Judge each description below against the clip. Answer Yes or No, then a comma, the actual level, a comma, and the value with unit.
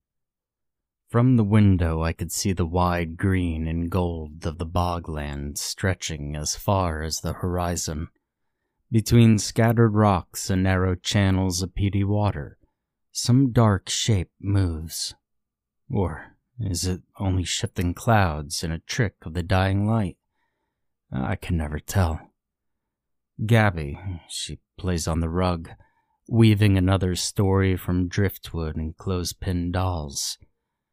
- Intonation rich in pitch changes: No, average, 3.5 semitones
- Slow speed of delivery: Yes, slow, 125 wpm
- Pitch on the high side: No, very low, 90 Hz